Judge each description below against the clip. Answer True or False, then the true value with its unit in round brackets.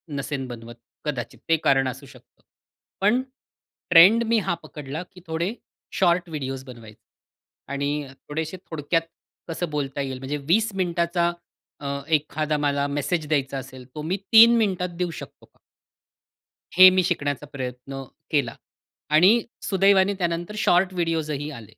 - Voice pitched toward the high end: False (155 Hz)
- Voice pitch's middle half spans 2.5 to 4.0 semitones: False (4.6 semitones)